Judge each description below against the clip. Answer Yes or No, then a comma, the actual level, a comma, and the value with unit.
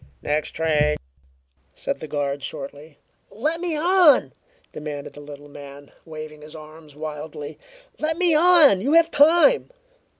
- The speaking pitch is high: No, medium, 155 Hz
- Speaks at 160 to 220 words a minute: No, slow, 135 wpm